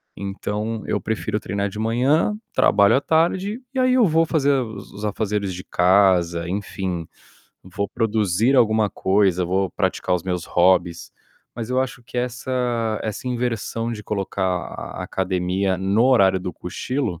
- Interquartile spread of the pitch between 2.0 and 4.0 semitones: No, average, 4.6 semitones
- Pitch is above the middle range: No, low, 105 Hz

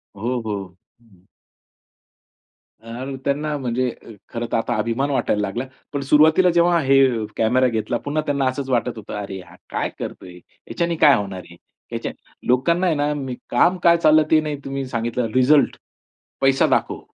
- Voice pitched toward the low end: Yes, low, 130 Hz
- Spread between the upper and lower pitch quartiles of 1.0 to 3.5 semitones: No, average, 4.2 semitones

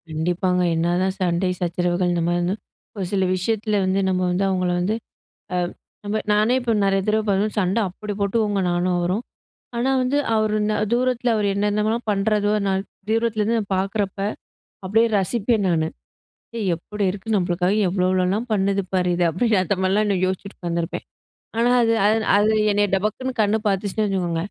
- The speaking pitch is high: Yes, high, 195 Hz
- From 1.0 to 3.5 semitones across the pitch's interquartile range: Yes, average, 2.8 semitones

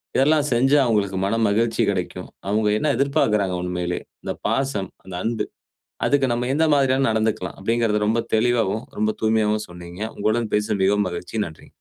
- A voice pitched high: No, low, 110 Hz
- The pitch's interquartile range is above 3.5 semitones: No, average, 3.1 semitones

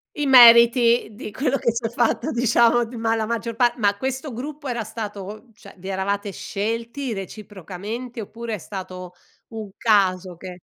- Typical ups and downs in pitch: Yes, average, 3.1 semitones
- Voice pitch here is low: No, high, 225 Hz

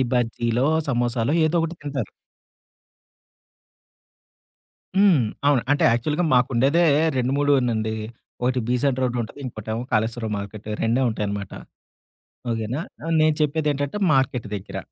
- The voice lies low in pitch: Yes, low, 125 Hz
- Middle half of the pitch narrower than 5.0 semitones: Yes, average, 4.0 semitones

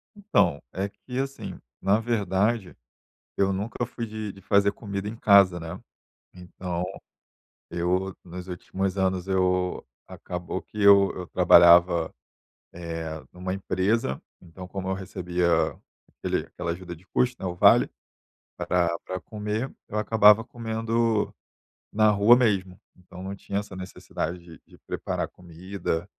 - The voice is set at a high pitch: No, very low, 95 Hz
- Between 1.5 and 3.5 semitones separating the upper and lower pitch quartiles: Yes, average, 2.8 semitones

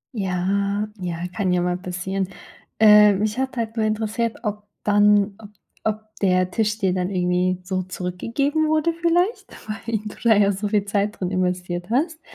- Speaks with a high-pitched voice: Yes, high, 205 Hz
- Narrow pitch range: No, average, 3.1 semitones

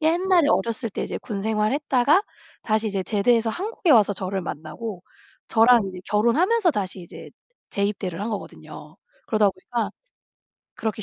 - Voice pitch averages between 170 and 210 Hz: No, high, 220 Hz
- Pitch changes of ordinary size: Yes, average, 4.2 semitones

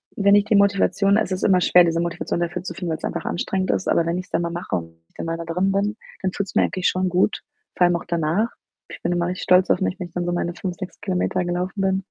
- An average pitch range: No, narrow, 2.0 semitones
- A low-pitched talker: No, medium, 180 Hz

